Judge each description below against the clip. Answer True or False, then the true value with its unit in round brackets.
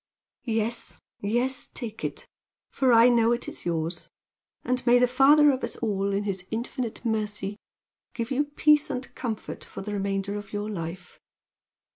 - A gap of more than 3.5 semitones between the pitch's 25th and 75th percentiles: True (4.0 semitones)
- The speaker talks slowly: False (160 wpm)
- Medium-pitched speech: False (225 Hz)